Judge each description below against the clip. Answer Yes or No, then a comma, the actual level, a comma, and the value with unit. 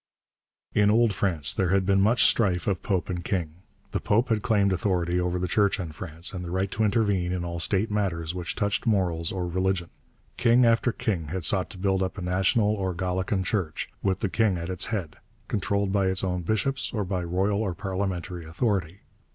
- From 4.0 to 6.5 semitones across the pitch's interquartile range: No, narrow, 2.5 semitones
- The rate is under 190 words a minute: No, fast, 205 wpm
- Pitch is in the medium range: No, very low, 95 Hz